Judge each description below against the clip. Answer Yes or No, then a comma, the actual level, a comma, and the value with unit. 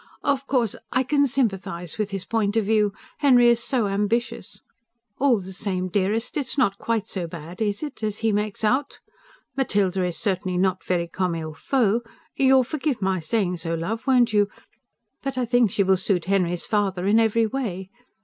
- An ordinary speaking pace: Yes, average, 185 wpm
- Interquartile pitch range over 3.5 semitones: Yes, average, 4.3 semitones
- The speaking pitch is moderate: No, high, 210 Hz